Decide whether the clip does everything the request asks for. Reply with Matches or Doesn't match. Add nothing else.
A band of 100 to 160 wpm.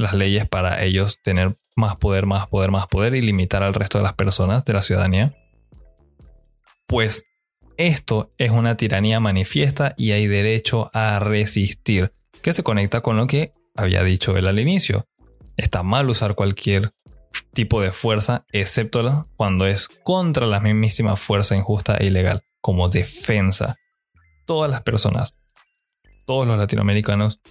Matches